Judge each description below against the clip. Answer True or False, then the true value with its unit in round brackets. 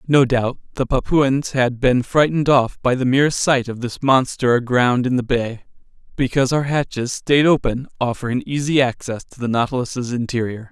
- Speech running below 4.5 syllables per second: False (5.0 syllables/s)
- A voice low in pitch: True (130 Hz)